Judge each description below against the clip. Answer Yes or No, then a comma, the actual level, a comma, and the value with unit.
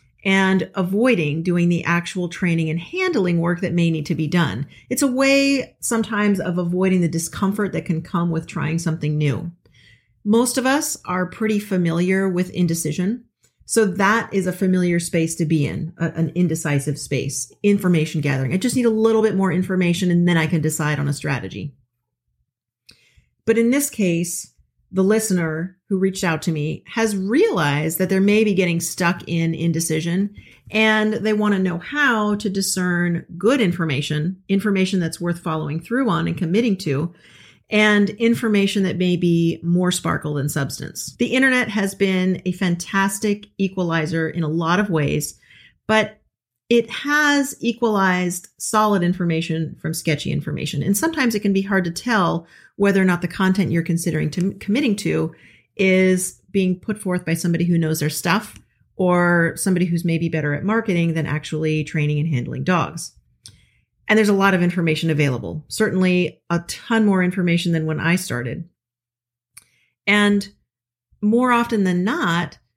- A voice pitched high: No, medium, 175 Hz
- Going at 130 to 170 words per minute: Yes, average, 165 wpm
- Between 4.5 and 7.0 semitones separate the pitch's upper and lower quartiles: No, average, 3.9 semitones